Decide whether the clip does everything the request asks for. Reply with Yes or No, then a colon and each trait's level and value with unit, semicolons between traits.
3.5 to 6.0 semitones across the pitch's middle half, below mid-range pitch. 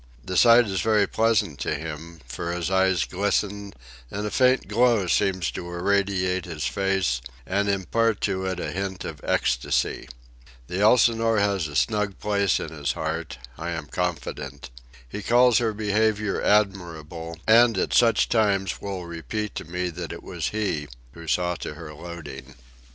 Yes: average, 4.0 semitones; very low, 95 Hz